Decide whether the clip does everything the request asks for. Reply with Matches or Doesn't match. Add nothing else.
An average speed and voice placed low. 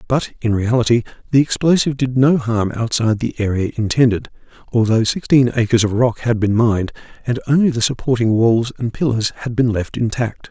Matches